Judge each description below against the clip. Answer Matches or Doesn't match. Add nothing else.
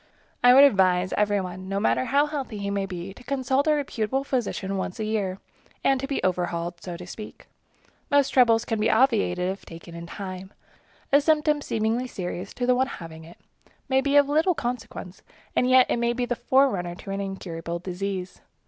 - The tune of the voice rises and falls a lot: Matches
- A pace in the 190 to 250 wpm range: Matches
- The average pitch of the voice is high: Matches